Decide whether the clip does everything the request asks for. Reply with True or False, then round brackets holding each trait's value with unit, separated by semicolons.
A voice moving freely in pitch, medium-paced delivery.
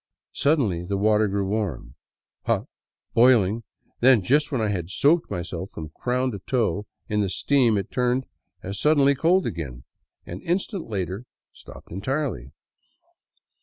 True (5.8 semitones; 145 wpm)